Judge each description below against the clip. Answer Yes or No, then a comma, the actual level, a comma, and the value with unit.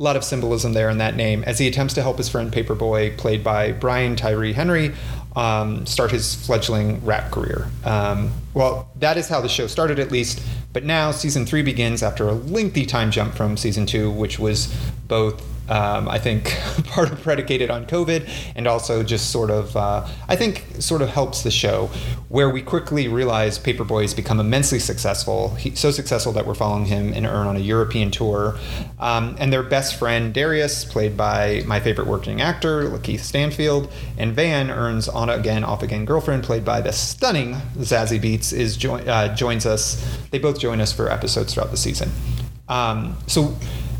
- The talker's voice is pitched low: Yes, low, 115 Hz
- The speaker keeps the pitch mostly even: No, average, 3.7 semitones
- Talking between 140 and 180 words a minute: No, average, 190 wpm